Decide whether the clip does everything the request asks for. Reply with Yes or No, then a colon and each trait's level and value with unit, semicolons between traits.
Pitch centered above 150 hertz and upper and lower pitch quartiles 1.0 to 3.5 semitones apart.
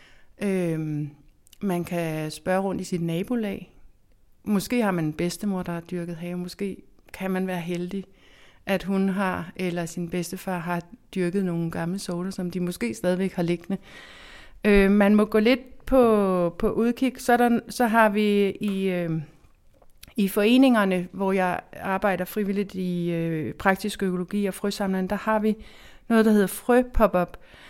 Yes: high, 190 Hz; average, 2.9 semitones